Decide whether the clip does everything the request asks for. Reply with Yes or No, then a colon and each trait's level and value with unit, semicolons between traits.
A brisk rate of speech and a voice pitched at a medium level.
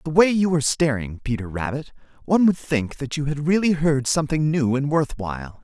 Yes: fast, 215 wpm; medium, 145 Hz